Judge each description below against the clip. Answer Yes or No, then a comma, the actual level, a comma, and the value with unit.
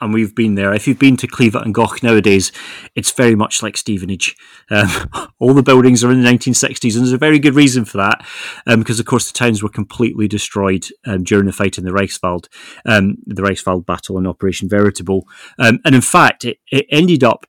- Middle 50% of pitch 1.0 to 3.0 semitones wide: No, average, 4.0 semitones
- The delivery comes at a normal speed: No, fast, 220 wpm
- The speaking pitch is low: Yes, low, 110 Hz